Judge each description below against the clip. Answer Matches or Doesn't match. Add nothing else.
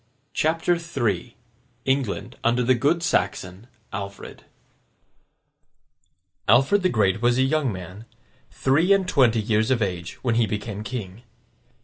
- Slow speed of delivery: Matches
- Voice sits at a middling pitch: Doesn't match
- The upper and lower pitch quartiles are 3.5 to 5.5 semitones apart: Matches